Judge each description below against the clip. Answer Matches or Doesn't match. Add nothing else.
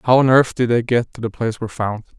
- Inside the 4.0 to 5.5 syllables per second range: Doesn't match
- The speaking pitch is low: Matches